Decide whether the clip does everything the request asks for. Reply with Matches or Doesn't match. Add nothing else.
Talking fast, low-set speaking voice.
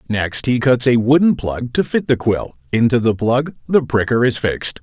Matches